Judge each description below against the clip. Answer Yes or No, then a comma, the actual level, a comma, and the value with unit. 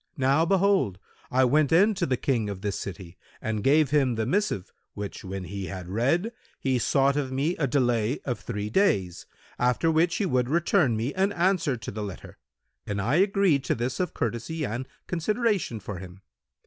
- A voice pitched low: Yes, low, 130 Hz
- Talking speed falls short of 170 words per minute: No, average, 185 wpm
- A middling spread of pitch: No, wide, 7.7 semitones